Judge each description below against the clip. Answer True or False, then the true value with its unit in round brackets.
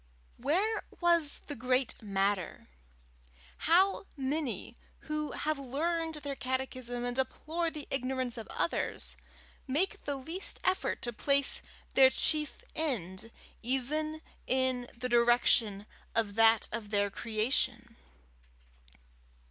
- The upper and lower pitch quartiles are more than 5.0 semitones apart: False (4.6 semitones)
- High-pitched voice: True (260 Hz)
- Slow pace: True (110 wpm)